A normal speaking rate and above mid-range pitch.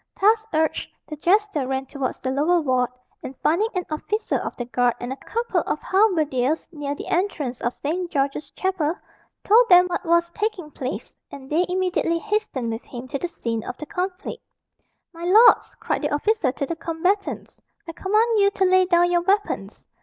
Yes: average, 185 wpm; very high, 340 Hz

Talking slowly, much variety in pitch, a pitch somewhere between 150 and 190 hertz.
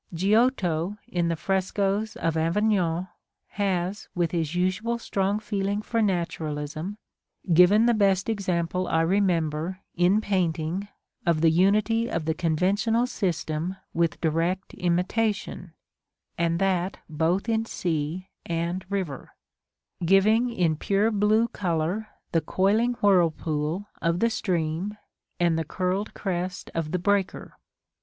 No: slow, 120 wpm; average, 3.6 semitones; medium, 185 Hz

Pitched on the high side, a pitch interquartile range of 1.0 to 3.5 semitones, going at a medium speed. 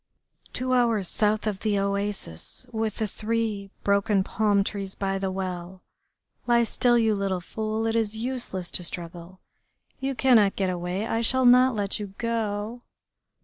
Yes: high, 210 Hz; average, 2.9 semitones; average, 155 wpm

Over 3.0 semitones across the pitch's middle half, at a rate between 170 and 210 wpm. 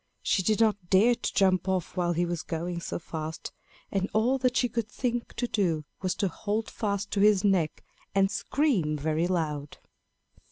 Yes: average, 4.1 semitones; average, 185 wpm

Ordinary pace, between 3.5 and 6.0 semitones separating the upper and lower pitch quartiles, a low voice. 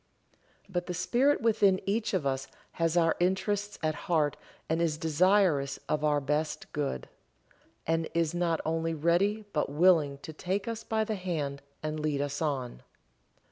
No: average, 160 wpm; average, 3.9 semitones; medium, 165 Hz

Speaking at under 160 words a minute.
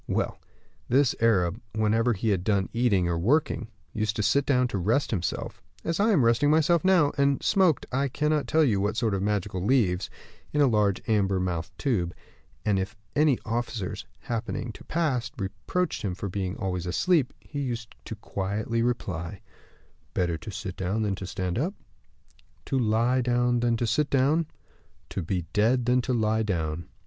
No: average, 175 wpm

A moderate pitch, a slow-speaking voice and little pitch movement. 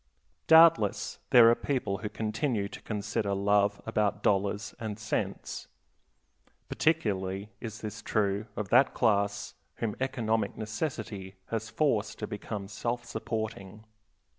No: low, 105 Hz; slow, 120 wpm; narrow, 2.1 semitones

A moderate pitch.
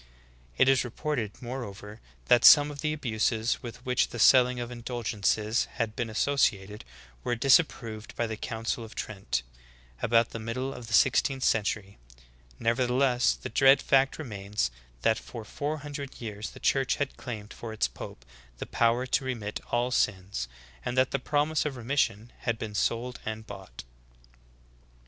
No: low, 120 Hz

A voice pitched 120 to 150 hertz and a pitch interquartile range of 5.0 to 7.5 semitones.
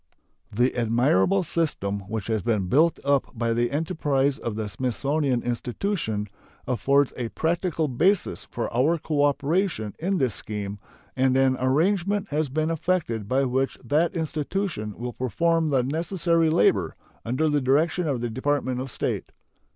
Yes: medium, 140 Hz; average, 5.3 semitones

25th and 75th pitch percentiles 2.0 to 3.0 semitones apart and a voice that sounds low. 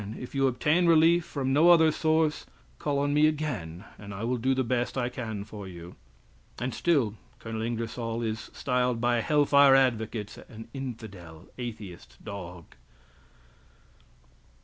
No: average, 4.6 semitones; low, 120 Hz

